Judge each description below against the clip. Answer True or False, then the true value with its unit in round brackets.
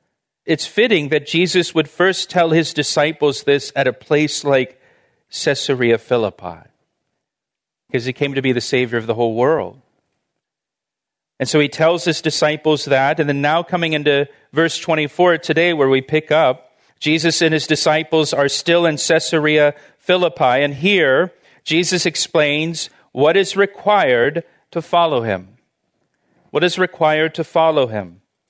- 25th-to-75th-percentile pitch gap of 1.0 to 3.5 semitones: True (3.0 semitones)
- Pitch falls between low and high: True (155 Hz)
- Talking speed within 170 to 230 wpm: False (150 wpm)